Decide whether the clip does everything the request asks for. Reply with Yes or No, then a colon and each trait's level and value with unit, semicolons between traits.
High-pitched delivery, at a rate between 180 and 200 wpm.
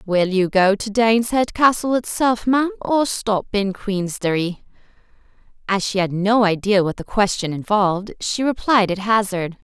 No: high, 210 Hz; average, 155 wpm